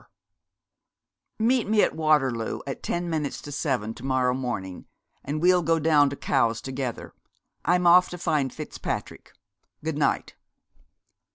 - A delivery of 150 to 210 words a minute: No, average, 140 wpm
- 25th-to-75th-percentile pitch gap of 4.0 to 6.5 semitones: Yes, average, 4.7 semitones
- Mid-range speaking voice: Yes, medium, 145 Hz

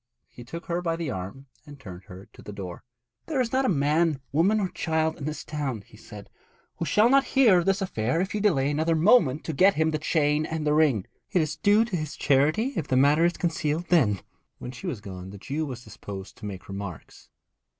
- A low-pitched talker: No, medium, 155 Hz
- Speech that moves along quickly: Yes, fast, 230 wpm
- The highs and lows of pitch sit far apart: Yes, wide, 5.9 semitones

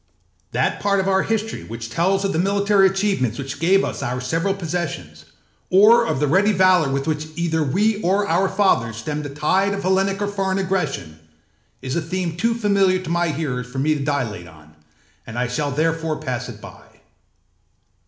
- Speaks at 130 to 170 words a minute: No, average, 190 wpm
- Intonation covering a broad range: Yes, wide, 6.2 semitones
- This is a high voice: No, medium, 170 Hz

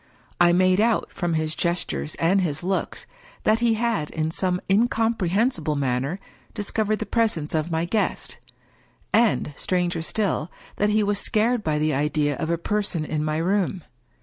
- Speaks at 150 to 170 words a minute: Yes, average, 165 wpm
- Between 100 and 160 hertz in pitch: No, medium, 180 Hz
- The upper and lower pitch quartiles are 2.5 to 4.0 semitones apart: No, average, 5.2 semitones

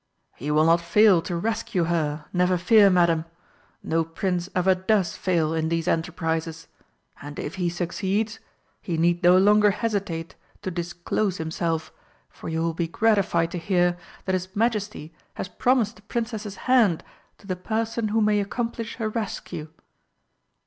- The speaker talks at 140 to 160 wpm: Yes, average, 155 wpm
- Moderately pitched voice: Yes, medium, 180 Hz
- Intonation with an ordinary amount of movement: Yes, average, 4.1 semitones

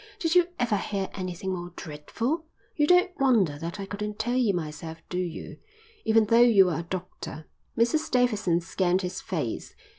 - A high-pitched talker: Yes, high, 195 Hz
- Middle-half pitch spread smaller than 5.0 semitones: No, wide, 5.6 semitones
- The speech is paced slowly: No, average, 175 wpm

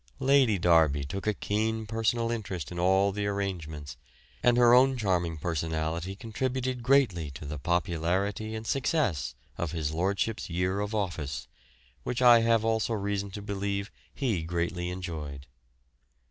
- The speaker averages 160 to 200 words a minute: No, average, 145 wpm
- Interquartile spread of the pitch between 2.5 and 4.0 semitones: No, average, 5.0 semitones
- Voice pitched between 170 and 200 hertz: No, low, 100 Hz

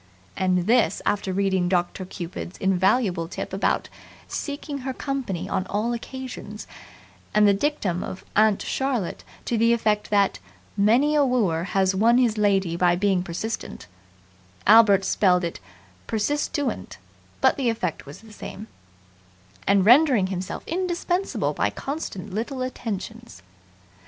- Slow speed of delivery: Yes, slow, 130 wpm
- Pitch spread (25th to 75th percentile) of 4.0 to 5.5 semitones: Yes, average, 4.9 semitones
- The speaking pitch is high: Yes, high, 205 Hz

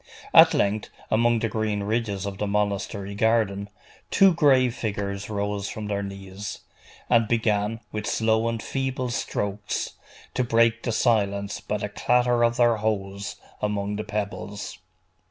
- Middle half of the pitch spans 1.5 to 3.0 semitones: Yes, narrow, 2.4 semitones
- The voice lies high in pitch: No, low, 105 Hz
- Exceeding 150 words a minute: No, average, 145 wpm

